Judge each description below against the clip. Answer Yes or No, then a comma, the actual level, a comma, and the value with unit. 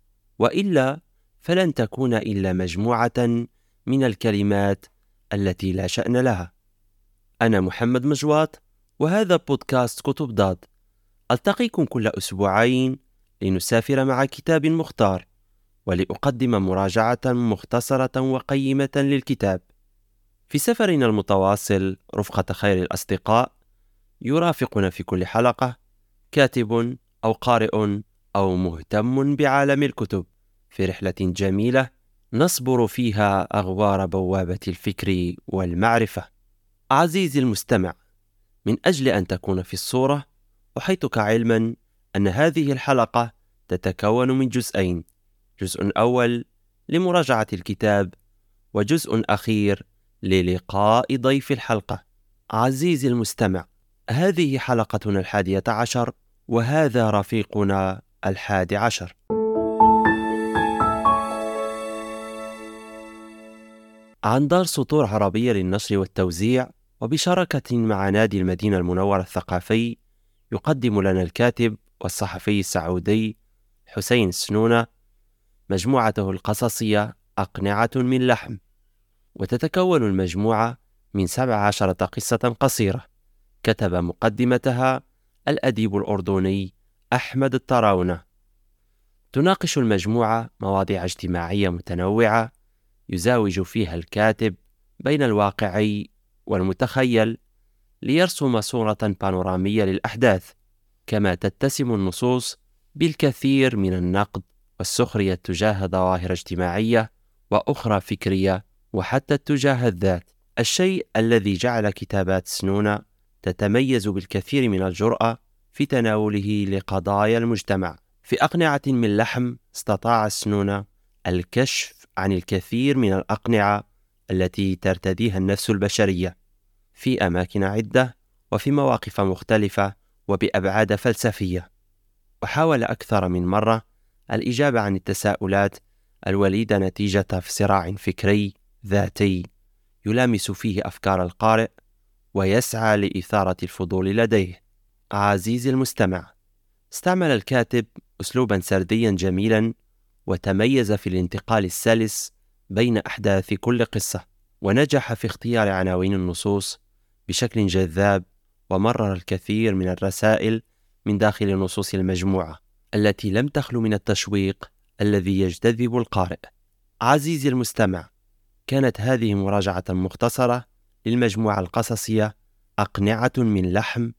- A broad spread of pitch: No, average, 3.3 semitones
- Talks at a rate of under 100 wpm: Yes, average, 90 wpm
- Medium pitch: No, low, 105 Hz